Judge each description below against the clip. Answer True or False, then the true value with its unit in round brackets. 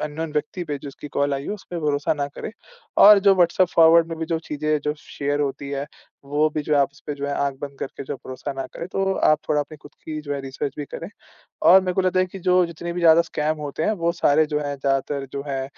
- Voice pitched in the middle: True (150 Hz)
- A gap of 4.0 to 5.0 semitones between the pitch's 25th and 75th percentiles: False (2.9 semitones)